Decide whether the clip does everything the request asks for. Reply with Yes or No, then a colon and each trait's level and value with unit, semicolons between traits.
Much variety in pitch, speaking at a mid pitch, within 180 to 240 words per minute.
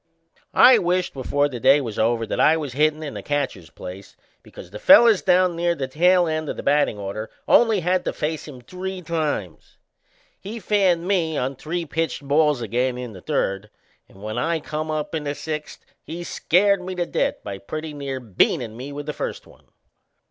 Yes: wide, 5.7 semitones; medium, 150 Hz; average, 200 wpm